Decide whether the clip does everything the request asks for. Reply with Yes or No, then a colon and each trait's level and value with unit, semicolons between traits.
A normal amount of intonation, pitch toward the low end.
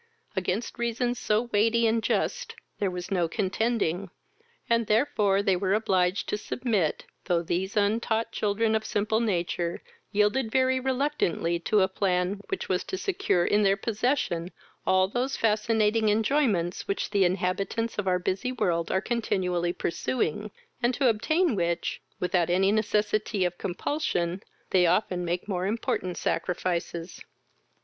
No: average, 4.0 semitones; high, 205 Hz